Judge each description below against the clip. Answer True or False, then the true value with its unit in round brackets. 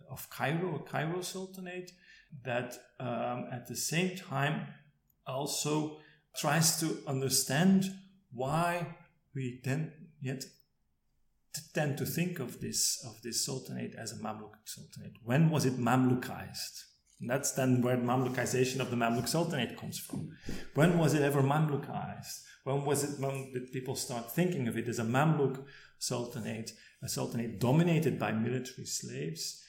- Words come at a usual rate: True (145 wpm)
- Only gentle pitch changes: False (4.2 semitones)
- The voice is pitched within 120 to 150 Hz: True (135 Hz)